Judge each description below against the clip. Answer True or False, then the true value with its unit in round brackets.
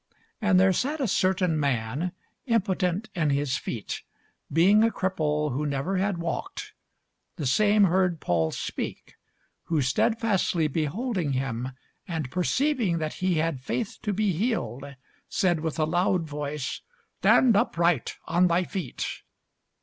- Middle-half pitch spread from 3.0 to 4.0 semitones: False (4.8 semitones)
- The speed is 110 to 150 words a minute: True (135 wpm)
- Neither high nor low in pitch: True (175 Hz)